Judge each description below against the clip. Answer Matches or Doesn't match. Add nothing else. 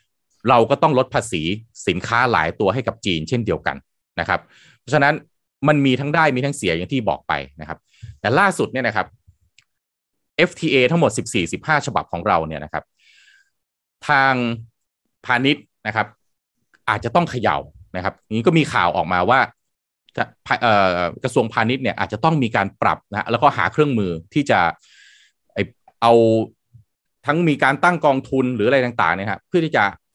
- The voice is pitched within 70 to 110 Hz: Doesn't match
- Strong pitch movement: Matches